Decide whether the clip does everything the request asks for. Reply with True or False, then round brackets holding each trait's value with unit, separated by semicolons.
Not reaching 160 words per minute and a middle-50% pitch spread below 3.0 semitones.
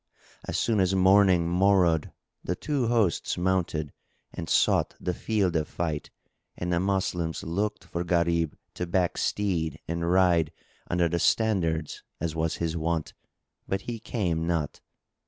True (145 wpm; 2.6 semitones)